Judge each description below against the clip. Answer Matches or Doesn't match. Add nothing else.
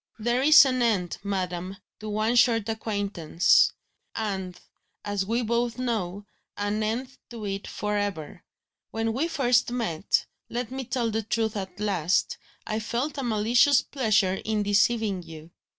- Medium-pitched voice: Doesn't match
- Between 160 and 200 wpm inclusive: Doesn't match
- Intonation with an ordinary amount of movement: Matches